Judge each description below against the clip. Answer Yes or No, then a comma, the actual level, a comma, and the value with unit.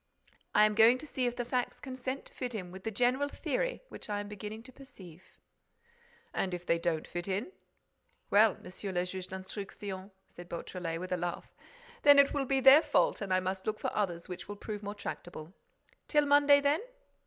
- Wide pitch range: Yes, wide, 5.7 semitones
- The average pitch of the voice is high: Yes, high, 205 Hz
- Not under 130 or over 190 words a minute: No, average, 200 wpm